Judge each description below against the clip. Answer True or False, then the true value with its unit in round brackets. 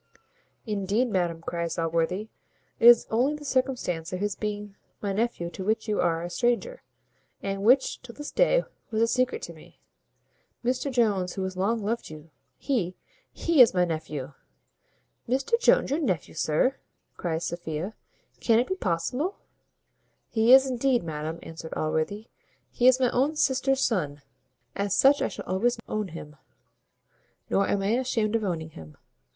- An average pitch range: False (6.7 semitones)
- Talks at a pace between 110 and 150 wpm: False (160 wpm)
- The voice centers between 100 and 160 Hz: False (210 Hz)